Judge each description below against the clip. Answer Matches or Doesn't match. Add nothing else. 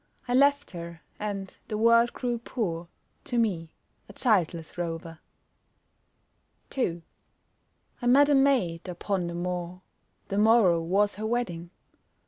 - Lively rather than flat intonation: Matches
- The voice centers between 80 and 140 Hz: Doesn't match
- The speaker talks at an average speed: Doesn't match